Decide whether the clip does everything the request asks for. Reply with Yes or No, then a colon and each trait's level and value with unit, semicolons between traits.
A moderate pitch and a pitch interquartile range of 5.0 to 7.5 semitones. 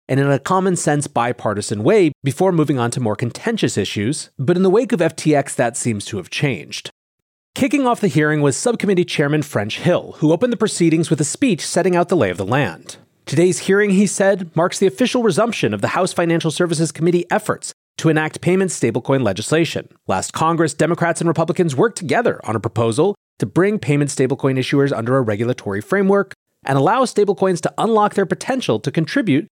Yes: medium, 165 Hz; wide, 5.6 semitones